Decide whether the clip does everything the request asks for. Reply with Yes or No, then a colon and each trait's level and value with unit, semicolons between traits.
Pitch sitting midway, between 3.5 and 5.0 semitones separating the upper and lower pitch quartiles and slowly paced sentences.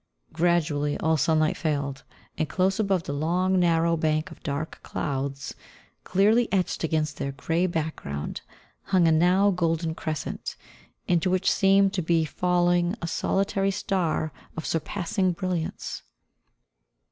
No: medium, 170 Hz; average, 3.0 semitones; slow, 130 wpm